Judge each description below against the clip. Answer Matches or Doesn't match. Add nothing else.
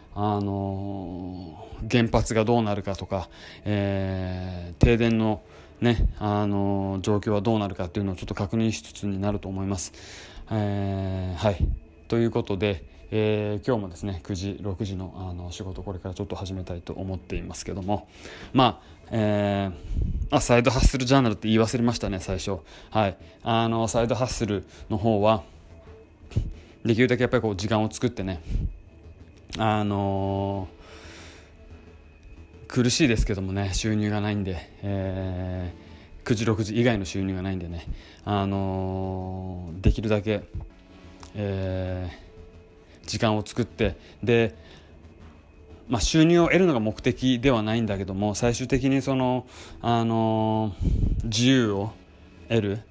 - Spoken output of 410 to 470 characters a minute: Doesn't match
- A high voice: Doesn't match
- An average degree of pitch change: Matches